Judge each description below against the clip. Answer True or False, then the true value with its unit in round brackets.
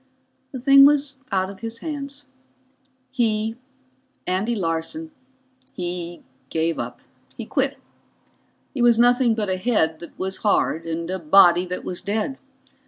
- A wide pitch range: True (6.0 semitones)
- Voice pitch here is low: False (210 Hz)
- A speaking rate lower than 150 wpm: True (140 wpm)